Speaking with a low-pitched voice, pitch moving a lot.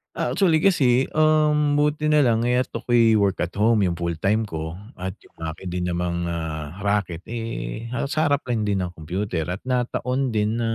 Yes: low, 110 Hz; wide, 6.3 semitones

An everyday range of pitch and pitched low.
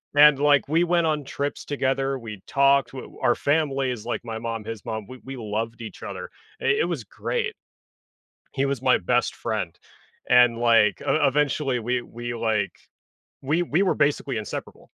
Yes: average, 4.0 semitones; low, 130 Hz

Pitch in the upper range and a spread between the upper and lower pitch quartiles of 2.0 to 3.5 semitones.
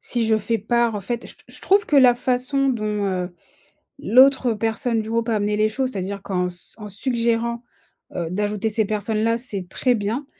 Yes: high, 225 Hz; average, 2.9 semitones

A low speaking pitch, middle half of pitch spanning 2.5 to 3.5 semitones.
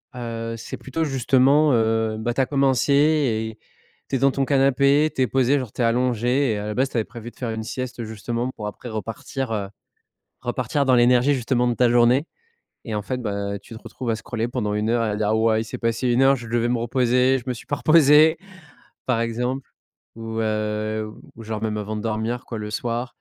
Yes: low, 120 Hz; average, 2.8 semitones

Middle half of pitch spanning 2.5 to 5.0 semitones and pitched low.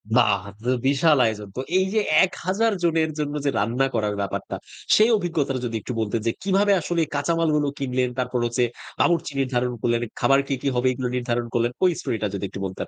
No: wide, 5.6 semitones; low, 130 Hz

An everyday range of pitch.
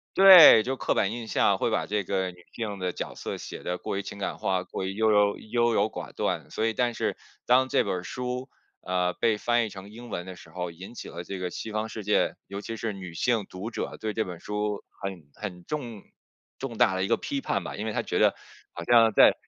Yes: average, 3.8 semitones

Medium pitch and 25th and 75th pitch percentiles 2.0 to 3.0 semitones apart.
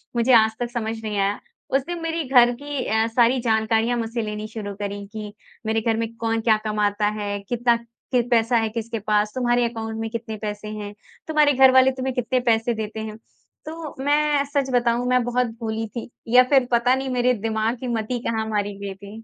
No: high, 230 Hz; narrow, 2.5 semitones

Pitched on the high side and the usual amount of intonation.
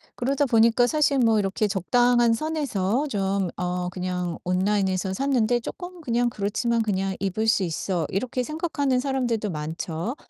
Yes: high, 220 Hz; average, 4.9 semitones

